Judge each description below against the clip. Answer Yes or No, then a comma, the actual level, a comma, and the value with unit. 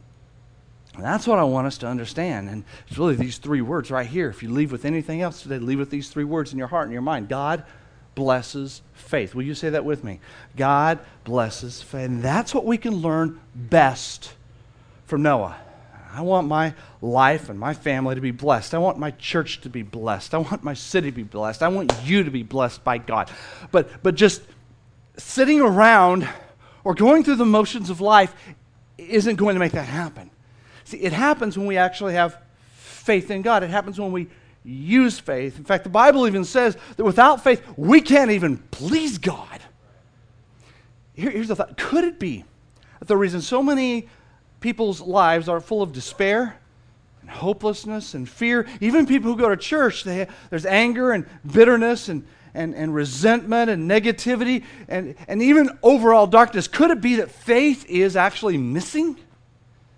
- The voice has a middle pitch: Yes, medium, 160 Hz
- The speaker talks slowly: No, average, 185 wpm